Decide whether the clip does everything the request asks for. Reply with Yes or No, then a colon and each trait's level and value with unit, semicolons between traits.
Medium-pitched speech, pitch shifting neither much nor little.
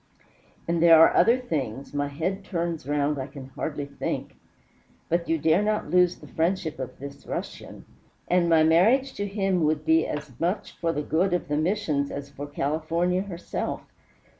Yes: medium, 160 Hz; average, 3.6 semitones